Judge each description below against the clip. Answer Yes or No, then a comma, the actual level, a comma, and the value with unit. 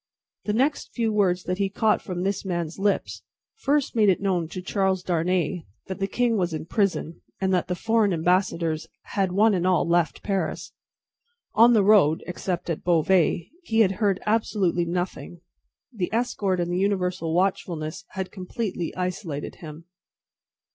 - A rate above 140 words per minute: Yes, average, 160 wpm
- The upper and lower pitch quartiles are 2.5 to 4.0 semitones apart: Yes, average, 2.9 semitones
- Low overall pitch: No, medium, 185 Hz